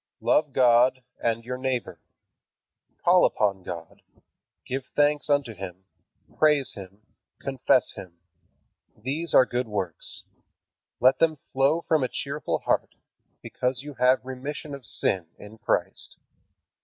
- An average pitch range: Yes, average, 4.7 semitones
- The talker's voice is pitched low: Yes, low, 130 Hz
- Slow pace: Yes, slow, 125 wpm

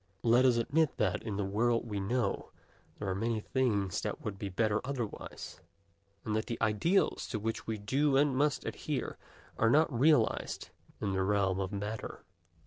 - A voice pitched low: Yes, low, 110 Hz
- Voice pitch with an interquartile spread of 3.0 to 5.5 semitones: Yes, average, 4.0 semitones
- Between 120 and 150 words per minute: No, average, 175 wpm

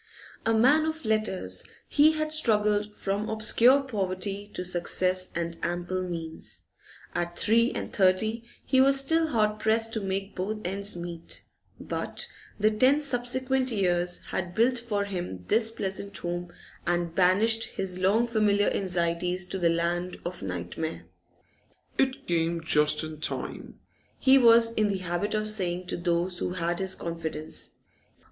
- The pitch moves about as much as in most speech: Yes, average, 4.4 semitones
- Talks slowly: No, average, 150 wpm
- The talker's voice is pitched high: Yes, high, 195 Hz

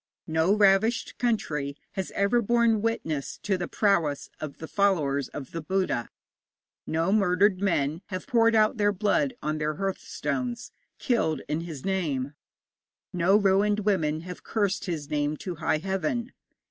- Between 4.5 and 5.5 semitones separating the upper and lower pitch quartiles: Yes, average, 5.2 semitones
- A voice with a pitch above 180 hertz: Yes, high, 190 Hz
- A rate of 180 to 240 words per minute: No, average, 145 wpm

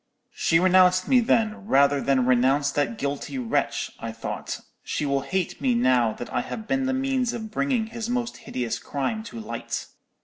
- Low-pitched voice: No, medium, 185 Hz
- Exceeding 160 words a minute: Yes, average, 180 wpm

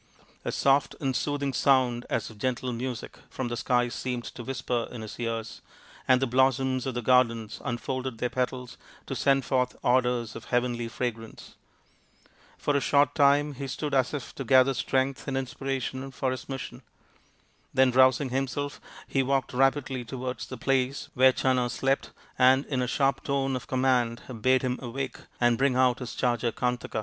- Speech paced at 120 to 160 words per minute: No, average, 175 wpm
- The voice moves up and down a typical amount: No, narrow, 1.7 semitones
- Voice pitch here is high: No, low, 130 Hz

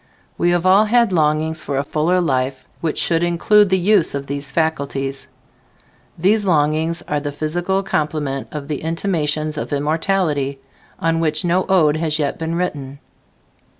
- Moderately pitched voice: Yes, medium, 160 Hz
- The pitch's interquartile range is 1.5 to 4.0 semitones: Yes, average, 3.2 semitones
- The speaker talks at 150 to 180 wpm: Yes, average, 155 wpm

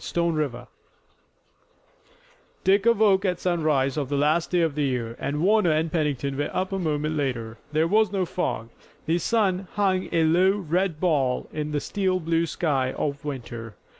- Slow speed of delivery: No, average, 170 wpm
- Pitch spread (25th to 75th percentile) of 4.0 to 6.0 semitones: Yes, average, 4.5 semitones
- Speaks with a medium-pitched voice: Yes, medium, 160 Hz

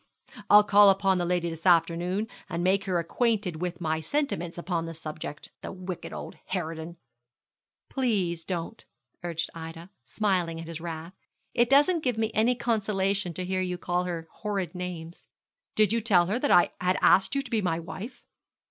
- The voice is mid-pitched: Yes, medium, 180 Hz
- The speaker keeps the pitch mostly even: No, average, 3.8 semitones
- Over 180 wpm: No, average, 175 wpm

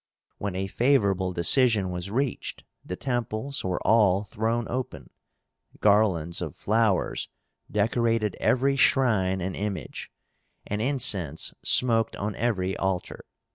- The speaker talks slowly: Yes, slow, 115 wpm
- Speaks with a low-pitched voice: Yes, low, 105 Hz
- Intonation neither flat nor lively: Yes, average, 4.1 semitones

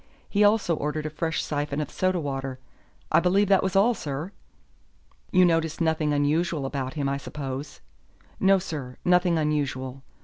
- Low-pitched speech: No, medium, 155 Hz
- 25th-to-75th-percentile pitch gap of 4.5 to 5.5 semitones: No, average, 4.1 semitones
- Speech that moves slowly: No, average, 160 wpm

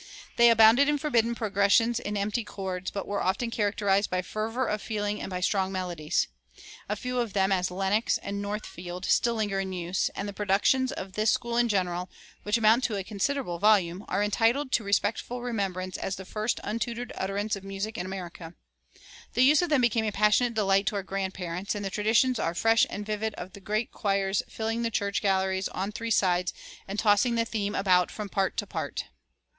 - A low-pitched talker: No, high, 205 Hz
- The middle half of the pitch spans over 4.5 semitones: No, average, 2.8 semitones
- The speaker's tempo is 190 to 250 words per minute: Yes, average, 200 wpm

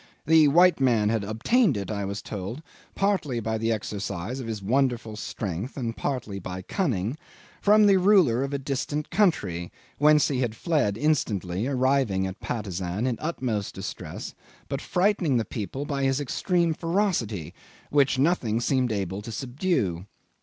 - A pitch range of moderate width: No, wide, 6.4 semitones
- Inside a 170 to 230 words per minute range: No, average, 155 wpm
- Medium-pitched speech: No, low, 125 Hz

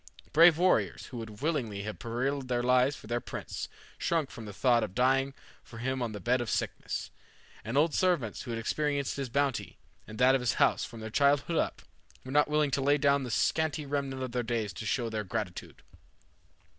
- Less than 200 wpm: No, fast, 205 wpm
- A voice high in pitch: No, low, 130 Hz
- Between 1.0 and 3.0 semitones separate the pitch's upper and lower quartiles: No, average, 3.7 semitones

